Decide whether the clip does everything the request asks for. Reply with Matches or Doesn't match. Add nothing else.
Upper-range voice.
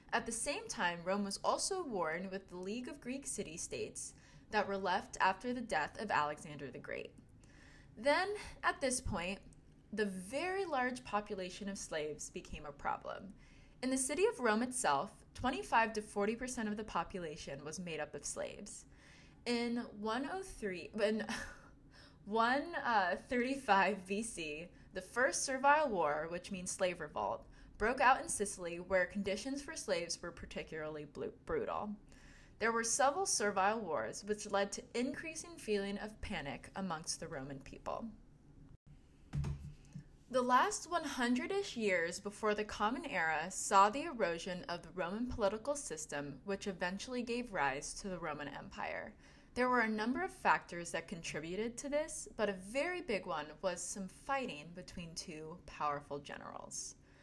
Matches